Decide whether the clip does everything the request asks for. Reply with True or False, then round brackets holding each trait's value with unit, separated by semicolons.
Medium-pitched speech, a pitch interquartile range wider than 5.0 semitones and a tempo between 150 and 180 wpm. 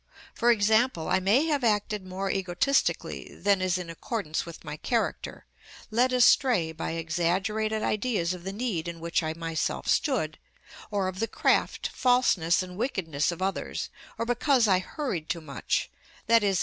False (195 Hz; 5.4 semitones; 160 wpm)